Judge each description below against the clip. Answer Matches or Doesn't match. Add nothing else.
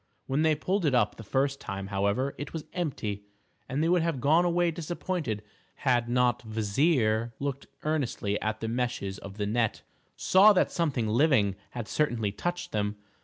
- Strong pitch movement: Matches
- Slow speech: Doesn't match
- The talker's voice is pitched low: Matches